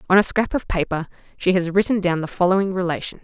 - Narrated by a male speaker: No, female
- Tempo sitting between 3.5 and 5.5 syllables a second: No, 6.5 syllables/s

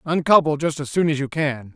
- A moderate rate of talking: No, fast, 240 wpm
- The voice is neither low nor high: Yes, medium, 150 Hz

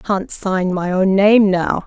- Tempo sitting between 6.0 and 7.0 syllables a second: No, 4.0 syllables/s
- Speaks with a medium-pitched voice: No, high, 195 Hz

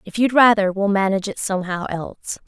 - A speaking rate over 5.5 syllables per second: Yes, 6.1 syllables/s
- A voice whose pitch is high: Yes, high, 200 Hz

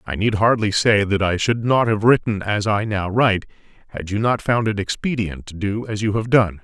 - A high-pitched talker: No, low, 105 Hz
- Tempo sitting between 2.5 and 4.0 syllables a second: No, 5.2 syllables/s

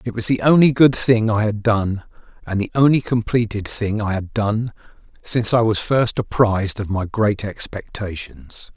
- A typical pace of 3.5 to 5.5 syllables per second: Yes, 4.6 syllables/s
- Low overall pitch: Yes, low, 110 Hz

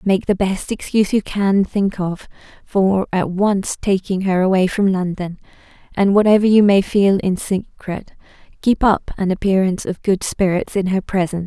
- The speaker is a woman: Yes, female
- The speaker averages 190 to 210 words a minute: No, average, 175 wpm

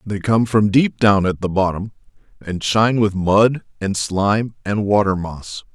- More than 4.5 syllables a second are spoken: No, 4.4 syllables/s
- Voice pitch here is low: Yes, low, 100 Hz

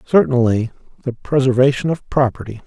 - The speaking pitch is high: No, low, 125 Hz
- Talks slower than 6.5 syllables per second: Yes, 5.8 syllables/s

